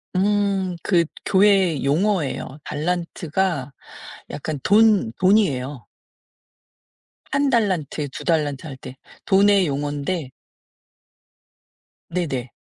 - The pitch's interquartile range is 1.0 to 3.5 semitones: No, wide, 5.5 semitones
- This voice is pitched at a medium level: Yes, medium, 170 Hz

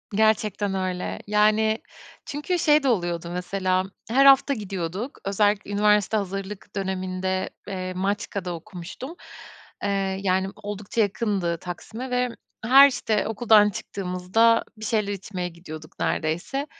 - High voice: Yes, high, 200 Hz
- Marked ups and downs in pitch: No, average, 3.1 semitones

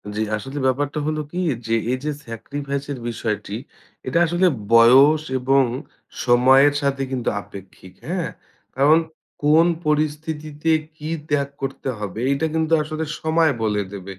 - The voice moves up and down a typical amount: Yes, average, 4.0 semitones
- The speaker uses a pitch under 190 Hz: Yes, medium, 140 Hz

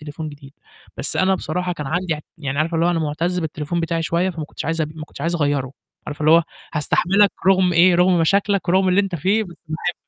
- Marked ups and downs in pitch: No, average, 2.9 semitones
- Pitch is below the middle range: No, medium, 170 Hz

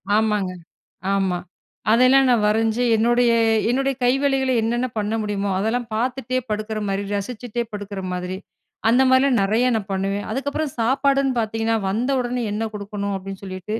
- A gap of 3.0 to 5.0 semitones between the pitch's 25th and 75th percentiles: Yes, average, 3.7 semitones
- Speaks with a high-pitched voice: Yes, high, 225 Hz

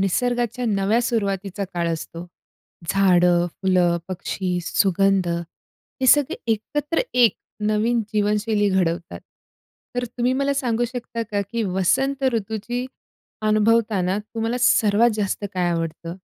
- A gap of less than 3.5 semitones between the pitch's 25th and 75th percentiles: No, average, 4.3 semitones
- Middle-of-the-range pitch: No, high, 210 Hz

